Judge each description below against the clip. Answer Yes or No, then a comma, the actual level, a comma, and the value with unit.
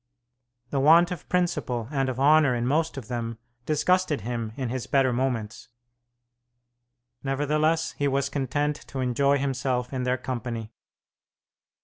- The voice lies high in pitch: No, low, 135 Hz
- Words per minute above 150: No, slow, 135 wpm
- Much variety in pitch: No, average, 3.1 semitones